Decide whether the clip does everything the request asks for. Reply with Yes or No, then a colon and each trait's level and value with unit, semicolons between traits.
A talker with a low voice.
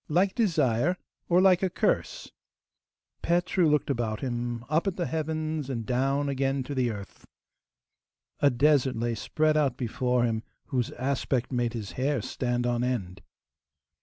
Yes: low, 130 Hz